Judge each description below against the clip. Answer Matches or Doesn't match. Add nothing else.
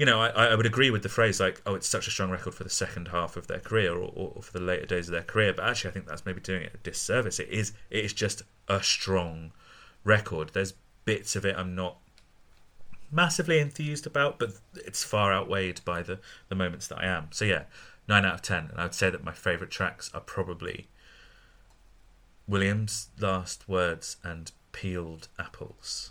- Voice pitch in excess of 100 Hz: Doesn't match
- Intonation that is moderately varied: Matches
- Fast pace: Matches